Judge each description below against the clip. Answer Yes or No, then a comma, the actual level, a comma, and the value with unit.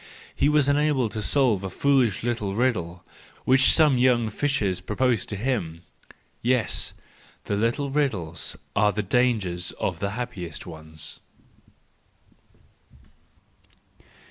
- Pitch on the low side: Yes, low, 115 Hz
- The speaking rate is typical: No, slow, 115 wpm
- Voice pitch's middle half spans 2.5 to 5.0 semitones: No, wide, 5.5 semitones